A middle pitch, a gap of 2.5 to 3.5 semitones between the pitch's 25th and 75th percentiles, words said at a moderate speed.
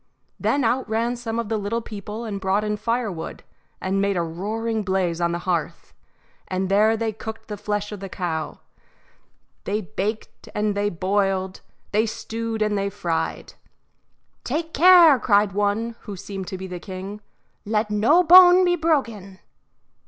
No: high, 210 Hz; average, 3.0 semitones; average, 160 wpm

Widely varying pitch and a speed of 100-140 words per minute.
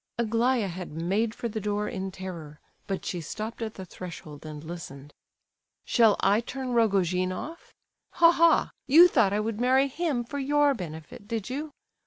No: wide, 5.8 semitones; average, 170 wpm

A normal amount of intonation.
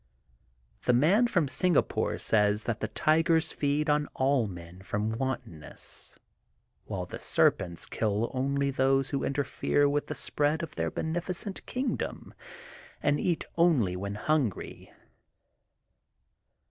No: wide, 6.4 semitones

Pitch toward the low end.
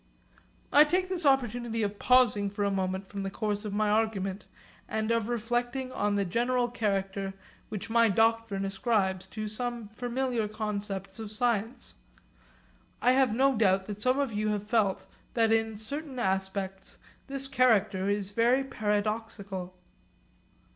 No: high, 215 Hz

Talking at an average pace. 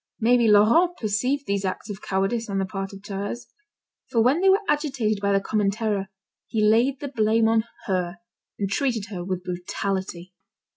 Yes: average, 180 wpm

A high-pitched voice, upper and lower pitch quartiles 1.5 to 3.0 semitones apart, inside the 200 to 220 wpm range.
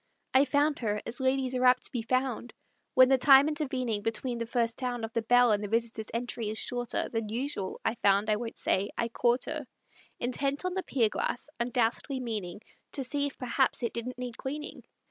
Yes: high, 245 Hz; average, 2.7 semitones; fast, 205 wpm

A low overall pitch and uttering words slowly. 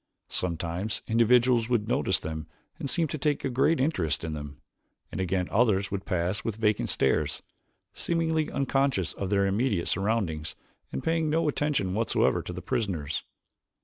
No: low, 105 Hz; average, 155 wpm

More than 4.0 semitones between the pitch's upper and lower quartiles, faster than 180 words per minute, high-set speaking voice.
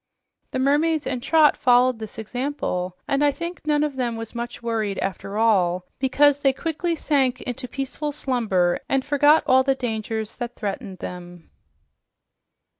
No: average, 4.7 semitones; average, 155 wpm; very high, 255 Hz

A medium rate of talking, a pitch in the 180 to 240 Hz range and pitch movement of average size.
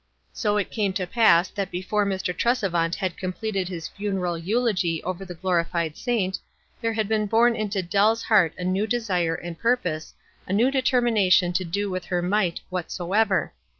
Yes: average, 170 wpm; high, 190 Hz; average, 3.4 semitones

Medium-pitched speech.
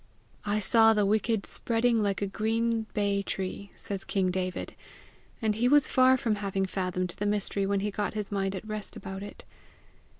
No: high, 205 Hz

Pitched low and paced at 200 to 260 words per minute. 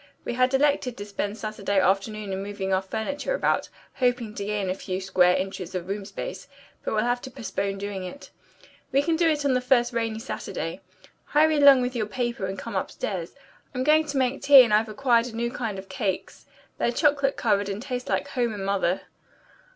No: high, 225 Hz; fast, 205 wpm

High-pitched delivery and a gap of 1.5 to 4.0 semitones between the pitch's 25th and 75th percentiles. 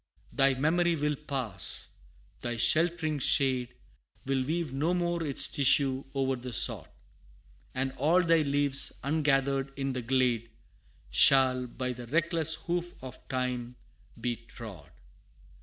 No: low, 135 Hz; average, 3.5 semitones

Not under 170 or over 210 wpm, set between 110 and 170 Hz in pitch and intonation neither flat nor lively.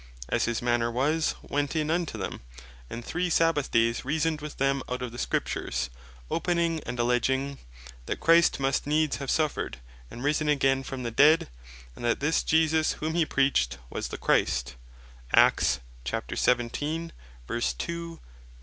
No: average, 140 wpm; medium, 140 Hz; average, 4.5 semitones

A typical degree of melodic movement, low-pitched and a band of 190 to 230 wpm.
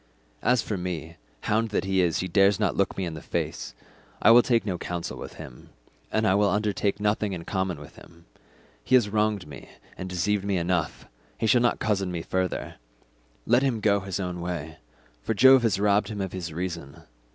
Yes: average, 3.3 semitones; very low, 95 Hz; average, 200 wpm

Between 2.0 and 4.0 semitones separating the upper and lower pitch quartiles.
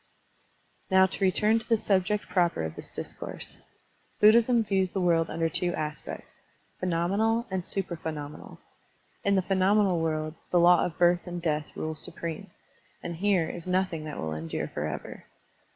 Yes: average, 3.0 semitones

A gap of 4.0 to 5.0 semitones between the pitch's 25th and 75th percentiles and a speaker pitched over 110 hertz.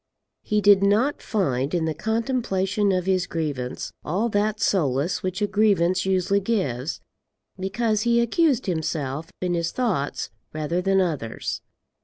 Yes: average, 4.6 semitones; high, 190 Hz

